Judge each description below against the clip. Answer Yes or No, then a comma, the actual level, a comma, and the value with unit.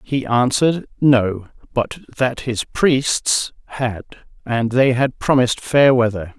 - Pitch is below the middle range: Yes, low, 125 Hz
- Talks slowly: Yes, slow, 130 wpm